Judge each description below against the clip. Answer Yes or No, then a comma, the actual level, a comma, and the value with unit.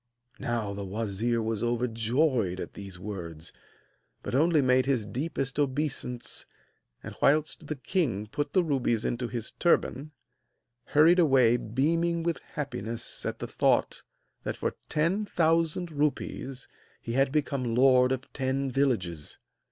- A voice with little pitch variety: No, average, 4.7 semitones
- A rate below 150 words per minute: Yes, slow, 135 wpm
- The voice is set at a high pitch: No, low, 130 Hz